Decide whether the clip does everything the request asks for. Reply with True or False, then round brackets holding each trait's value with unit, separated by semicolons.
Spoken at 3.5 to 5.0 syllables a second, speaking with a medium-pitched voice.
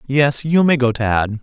False (3.9 syllables/s; 130 Hz)